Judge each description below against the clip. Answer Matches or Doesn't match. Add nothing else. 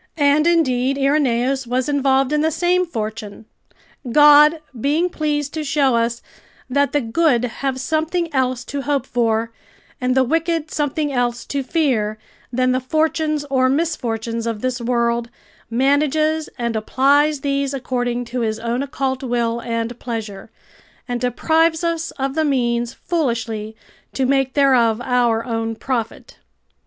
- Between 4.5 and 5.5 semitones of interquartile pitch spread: Doesn't match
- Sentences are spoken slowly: Doesn't match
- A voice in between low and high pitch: Doesn't match